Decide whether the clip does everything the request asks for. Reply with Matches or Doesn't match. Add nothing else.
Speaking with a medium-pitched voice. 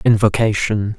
Doesn't match